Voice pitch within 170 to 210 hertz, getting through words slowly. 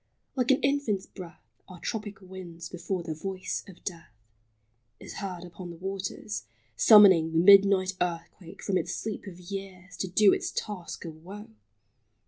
No: medium, 185 Hz; average, 155 wpm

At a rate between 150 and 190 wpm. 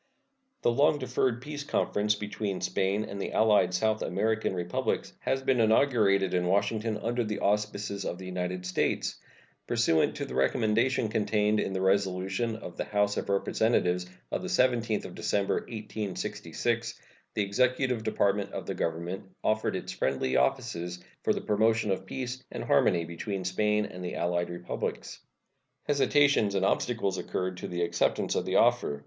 Yes: average, 160 wpm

